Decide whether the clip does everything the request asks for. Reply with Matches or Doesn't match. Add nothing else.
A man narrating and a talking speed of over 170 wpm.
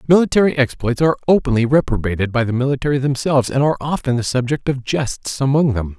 Matches